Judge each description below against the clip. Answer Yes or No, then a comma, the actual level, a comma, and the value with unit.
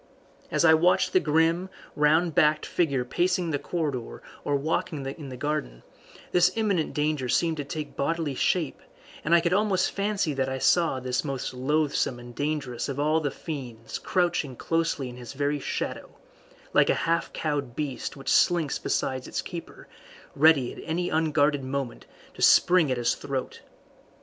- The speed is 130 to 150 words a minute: No, average, 165 wpm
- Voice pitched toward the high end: No, medium, 150 Hz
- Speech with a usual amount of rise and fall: Yes, average, 3.6 semitones